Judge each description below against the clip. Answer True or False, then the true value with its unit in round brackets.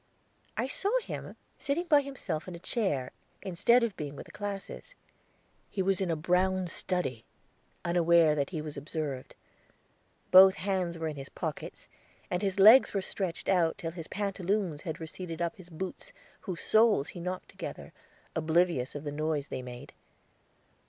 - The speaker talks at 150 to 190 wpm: True (165 wpm)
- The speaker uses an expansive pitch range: False (3.8 semitones)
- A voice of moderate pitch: True (175 Hz)